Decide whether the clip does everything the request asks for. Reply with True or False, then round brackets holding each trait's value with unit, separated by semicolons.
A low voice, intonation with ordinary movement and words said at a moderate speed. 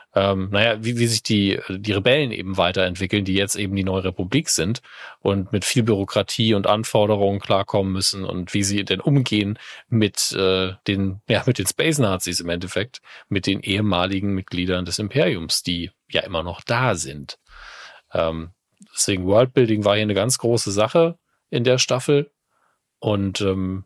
True (100 Hz; 3.3 semitones; 165 wpm)